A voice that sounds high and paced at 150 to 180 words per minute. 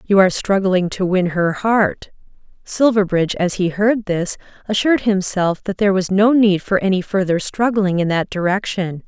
Yes: high, 195 Hz; average, 170 wpm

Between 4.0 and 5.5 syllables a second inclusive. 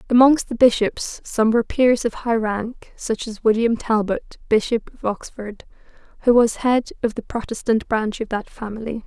Yes: 4.6 syllables/s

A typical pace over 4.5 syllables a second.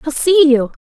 Yes: 4.7 syllables/s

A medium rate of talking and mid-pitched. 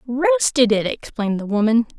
No: average, 150 wpm; high, 215 Hz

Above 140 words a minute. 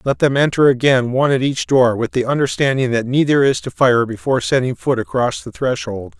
Yes: fast, 205 wpm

